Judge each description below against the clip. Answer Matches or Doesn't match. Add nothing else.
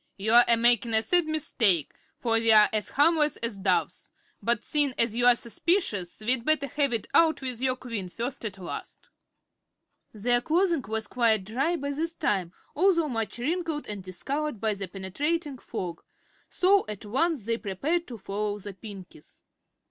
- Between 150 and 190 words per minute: Matches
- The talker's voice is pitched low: Doesn't match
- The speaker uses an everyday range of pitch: Doesn't match